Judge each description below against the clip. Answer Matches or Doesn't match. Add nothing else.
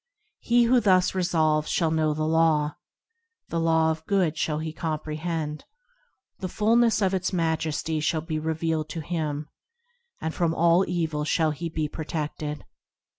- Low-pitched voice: Doesn't match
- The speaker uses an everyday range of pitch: Doesn't match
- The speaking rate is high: Doesn't match